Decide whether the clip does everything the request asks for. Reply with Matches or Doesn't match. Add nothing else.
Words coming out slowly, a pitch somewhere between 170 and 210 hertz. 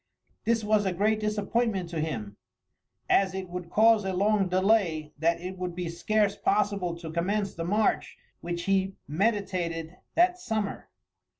Doesn't match